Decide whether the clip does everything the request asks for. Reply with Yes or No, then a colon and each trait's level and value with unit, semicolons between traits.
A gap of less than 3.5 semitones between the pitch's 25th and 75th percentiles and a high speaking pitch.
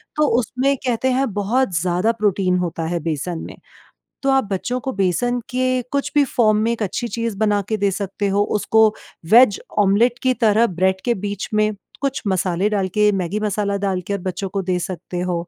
No: average, 4.0 semitones; high, 205 Hz